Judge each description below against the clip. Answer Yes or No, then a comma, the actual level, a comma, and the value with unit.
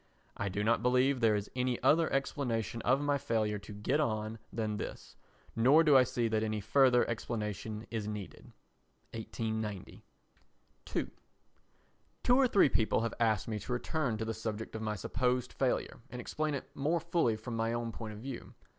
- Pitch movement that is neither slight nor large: Yes, average, 3.3 semitones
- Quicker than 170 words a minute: Yes, average, 180 wpm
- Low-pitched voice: Yes, low, 115 Hz